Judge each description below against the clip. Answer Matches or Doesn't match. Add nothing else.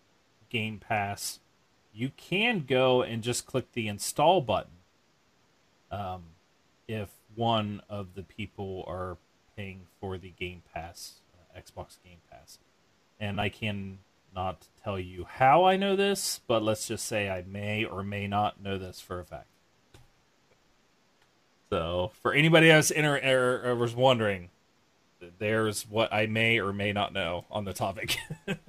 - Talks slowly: Doesn't match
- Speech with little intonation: Doesn't match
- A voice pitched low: Matches